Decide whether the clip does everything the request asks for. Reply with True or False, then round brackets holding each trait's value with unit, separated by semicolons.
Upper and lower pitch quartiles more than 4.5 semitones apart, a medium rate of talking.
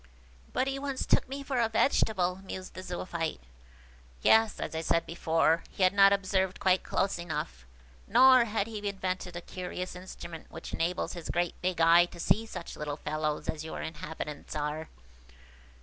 False (3.7 semitones; 175 wpm)